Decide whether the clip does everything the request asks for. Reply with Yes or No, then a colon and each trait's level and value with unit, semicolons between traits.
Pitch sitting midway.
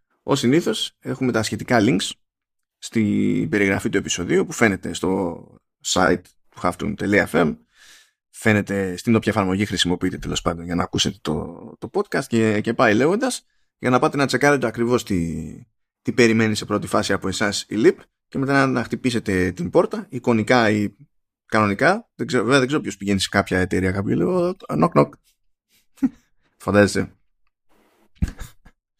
No: low, 110 Hz